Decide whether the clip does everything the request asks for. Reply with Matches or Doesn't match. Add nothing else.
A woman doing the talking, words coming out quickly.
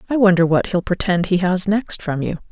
Matches